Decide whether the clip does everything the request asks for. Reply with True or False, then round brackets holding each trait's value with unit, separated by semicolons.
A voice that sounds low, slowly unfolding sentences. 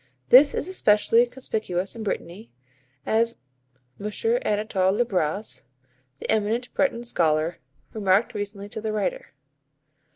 False (215 Hz; 120 wpm)